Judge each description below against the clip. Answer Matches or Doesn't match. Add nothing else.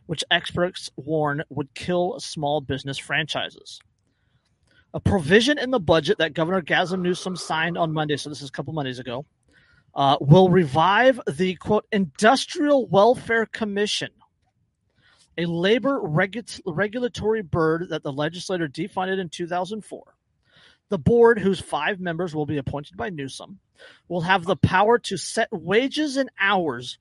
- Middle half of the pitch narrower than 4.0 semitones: Doesn't match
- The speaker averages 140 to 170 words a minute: Matches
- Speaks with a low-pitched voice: Doesn't match